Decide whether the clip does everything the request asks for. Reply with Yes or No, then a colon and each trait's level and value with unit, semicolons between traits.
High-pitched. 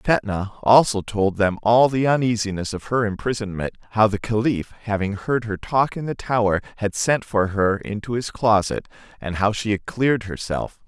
No: low, 110 Hz